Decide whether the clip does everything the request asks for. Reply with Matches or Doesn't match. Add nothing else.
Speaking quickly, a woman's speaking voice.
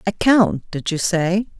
Doesn't match